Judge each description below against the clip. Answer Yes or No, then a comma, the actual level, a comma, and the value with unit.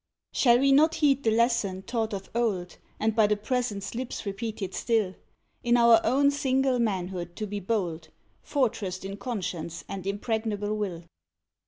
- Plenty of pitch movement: No, average, 3.7 semitones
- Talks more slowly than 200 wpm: Yes, average, 155 wpm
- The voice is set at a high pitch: Yes, high, 215 Hz